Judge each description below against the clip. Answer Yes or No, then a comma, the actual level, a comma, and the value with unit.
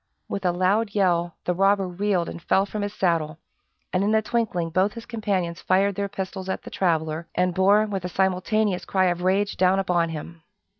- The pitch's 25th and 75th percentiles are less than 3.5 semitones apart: Yes, narrow, 2.5 semitones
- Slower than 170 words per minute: No, average, 200 wpm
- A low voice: No, high, 190 Hz